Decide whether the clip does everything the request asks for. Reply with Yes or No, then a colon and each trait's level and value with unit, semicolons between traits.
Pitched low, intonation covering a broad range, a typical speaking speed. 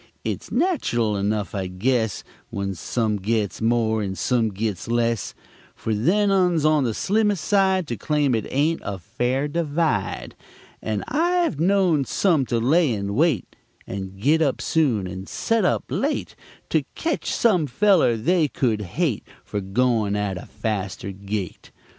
Yes: low, 120 Hz; wide, 8.0 semitones; average, 155 wpm